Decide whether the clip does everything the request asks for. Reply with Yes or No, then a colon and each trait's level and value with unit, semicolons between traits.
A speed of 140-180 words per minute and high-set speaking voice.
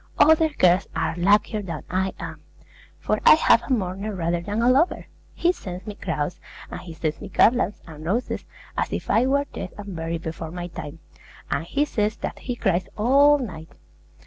No: average, 190 wpm; high, 195 Hz